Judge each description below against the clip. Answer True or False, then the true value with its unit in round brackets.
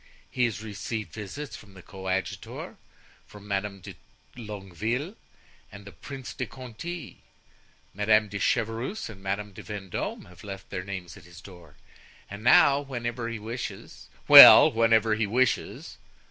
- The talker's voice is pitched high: False (105 Hz)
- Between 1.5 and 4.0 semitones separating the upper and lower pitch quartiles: True (3.3 semitones)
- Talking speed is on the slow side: False (145 wpm)